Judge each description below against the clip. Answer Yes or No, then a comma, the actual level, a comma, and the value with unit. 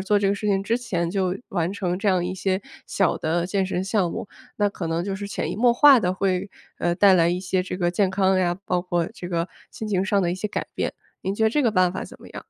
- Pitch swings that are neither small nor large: No, narrow, 2.2 semitones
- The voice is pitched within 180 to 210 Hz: Yes, high, 190 Hz